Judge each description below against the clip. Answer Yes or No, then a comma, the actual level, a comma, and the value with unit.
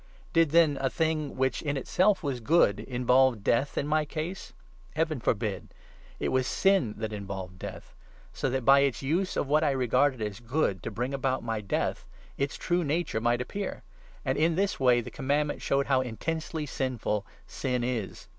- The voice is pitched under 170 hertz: Yes, low, 135 Hz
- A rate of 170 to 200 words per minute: Yes, average, 185 wpm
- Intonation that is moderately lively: Yes, average, 4.5 semitones